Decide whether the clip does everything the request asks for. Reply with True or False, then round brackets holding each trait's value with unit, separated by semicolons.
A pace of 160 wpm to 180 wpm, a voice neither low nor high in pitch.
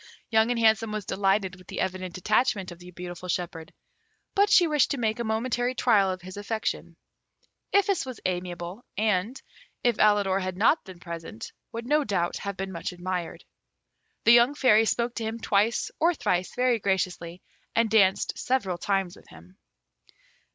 False (170 wpm; 205 Hz)